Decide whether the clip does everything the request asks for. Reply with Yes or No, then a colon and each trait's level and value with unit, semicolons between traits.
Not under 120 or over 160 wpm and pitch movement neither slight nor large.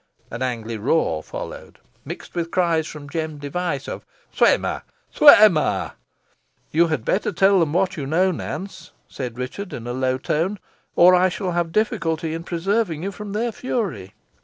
No: average, 170 wpm; average, 4.9 semitones